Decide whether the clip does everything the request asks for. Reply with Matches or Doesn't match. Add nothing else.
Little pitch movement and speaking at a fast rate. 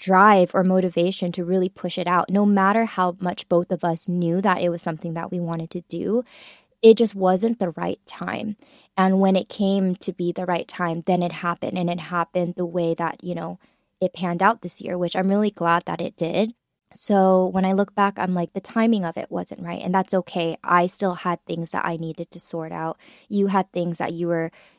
Matches